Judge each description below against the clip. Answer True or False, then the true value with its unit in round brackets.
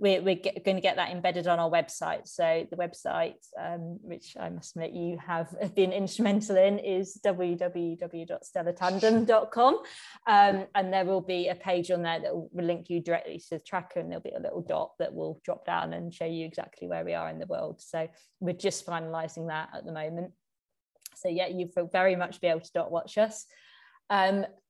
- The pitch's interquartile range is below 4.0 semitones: True (2.4 semitones)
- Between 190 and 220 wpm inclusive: True (200 wpm)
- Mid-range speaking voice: True (180 Hz)